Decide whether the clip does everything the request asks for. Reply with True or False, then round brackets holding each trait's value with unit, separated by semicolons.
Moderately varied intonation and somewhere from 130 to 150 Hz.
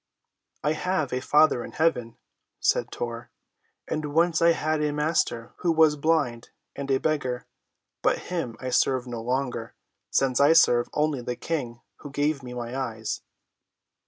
True (4.1 semitones; 140 Hz)